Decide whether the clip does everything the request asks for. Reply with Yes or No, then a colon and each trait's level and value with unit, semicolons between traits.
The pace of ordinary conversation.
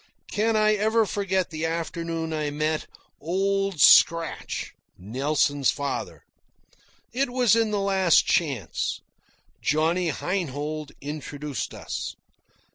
No: slow, 105 wpm